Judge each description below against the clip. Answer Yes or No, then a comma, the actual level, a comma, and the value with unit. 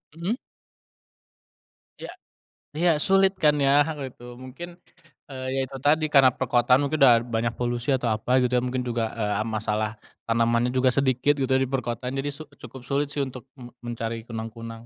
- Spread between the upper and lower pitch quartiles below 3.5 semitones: Yes, average, 2.9 semitones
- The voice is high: No, low, 125 Hz